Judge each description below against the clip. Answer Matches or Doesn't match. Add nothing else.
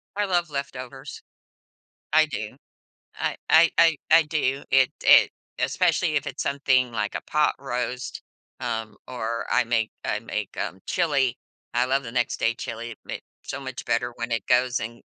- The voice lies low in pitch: Matches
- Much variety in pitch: Doesn't match